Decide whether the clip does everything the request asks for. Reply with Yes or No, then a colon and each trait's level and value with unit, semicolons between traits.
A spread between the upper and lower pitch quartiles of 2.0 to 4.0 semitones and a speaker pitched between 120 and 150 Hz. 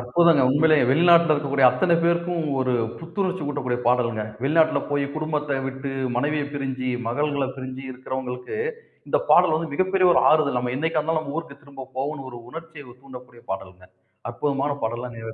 Yes: average, 3.7 semitones; medium, 140 Hz